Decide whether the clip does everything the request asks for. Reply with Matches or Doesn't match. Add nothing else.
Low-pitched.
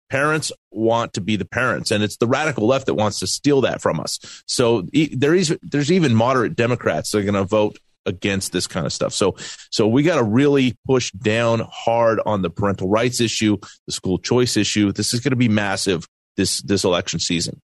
Matches